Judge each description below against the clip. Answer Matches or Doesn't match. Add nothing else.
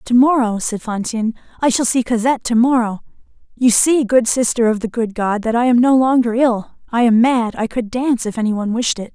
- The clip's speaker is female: Matches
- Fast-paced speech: Matches